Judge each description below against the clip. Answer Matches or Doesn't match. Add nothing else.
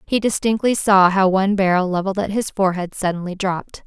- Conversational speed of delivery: Matches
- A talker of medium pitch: Doesn't match